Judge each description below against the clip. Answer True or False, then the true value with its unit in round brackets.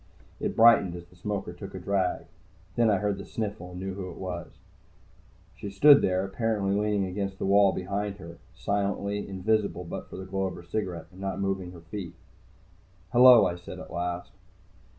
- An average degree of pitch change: False (2.2 semitones)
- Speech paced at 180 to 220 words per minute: True (190 wpm)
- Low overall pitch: True (95 Hz)